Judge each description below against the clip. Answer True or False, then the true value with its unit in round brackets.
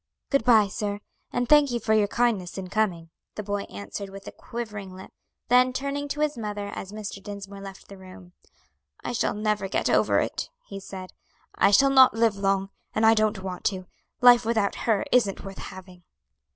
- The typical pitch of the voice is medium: False (205 Hz)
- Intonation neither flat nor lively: True (3.3 semitones)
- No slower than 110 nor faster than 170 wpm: False (190 wpm)